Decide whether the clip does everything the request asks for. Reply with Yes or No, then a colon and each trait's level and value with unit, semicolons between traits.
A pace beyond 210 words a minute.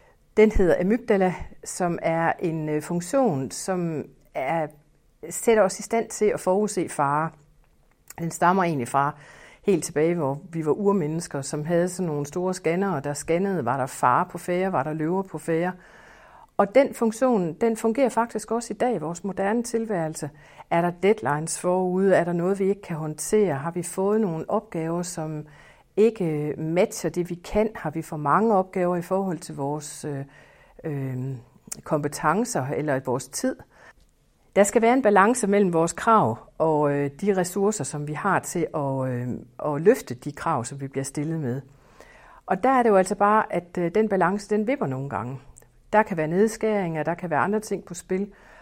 No: average, 185 wpm